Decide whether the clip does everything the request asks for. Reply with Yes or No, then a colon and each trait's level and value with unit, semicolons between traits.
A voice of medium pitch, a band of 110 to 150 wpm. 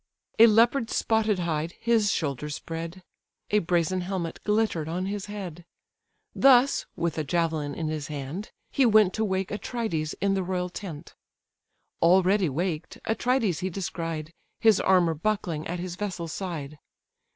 Yes: medium, 180 Hz; average, 145 wpm